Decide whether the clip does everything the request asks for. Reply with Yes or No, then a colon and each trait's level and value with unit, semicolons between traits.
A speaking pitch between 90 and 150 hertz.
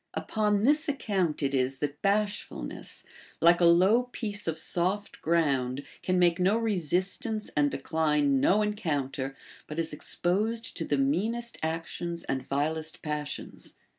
No: medium, 170 Hz